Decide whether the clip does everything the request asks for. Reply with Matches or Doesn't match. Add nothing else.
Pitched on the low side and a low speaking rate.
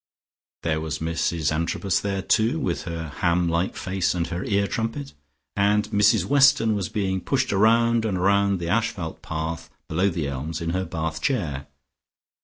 Doesn't match